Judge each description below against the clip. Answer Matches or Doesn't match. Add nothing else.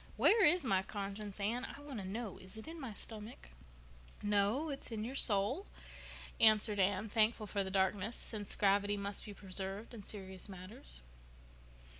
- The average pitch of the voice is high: Matches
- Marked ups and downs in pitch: Doesn't match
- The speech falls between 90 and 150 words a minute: Doesn't match